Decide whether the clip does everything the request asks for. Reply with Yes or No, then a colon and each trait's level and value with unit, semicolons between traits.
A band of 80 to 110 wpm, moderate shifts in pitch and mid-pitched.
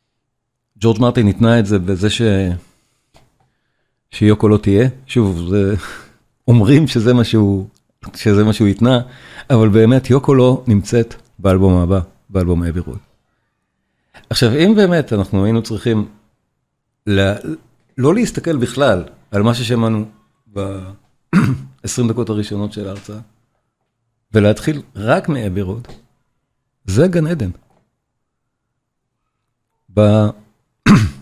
No: average, 105 wpm; average, 3.4 semitones; low, 115 Hz